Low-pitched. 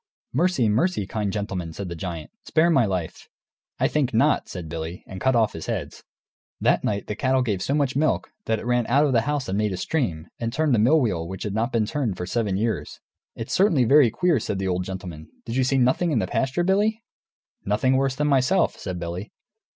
Yes: low, 115 Hz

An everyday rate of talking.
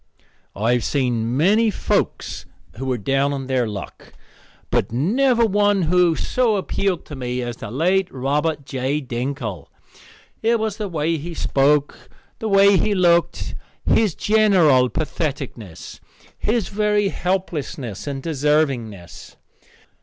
No: slow, 130 wpm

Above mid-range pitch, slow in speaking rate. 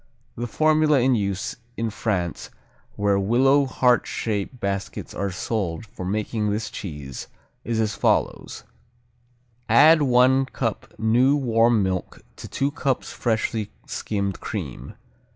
No: low, 110 Hz; slow, 125 wpm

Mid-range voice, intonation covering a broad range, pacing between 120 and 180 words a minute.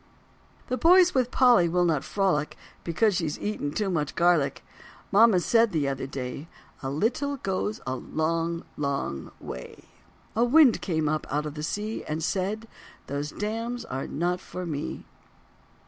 Yes: medium, 175 Hz; wide, 6.7 semitones; average, 155 wpm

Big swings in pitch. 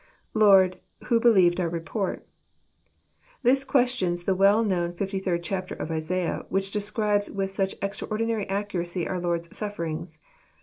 No: average, 3.1 semitones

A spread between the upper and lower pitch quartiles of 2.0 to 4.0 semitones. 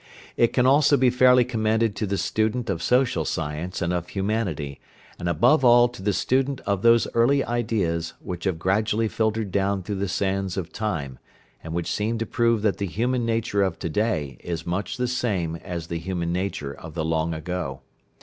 No: wide, 5.4 semitones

